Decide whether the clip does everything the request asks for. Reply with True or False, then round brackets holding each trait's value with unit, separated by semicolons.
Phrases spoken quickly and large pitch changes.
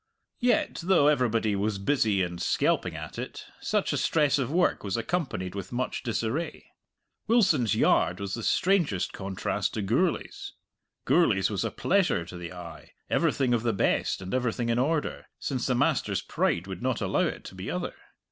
False (175 wpm; 7.2 semitones)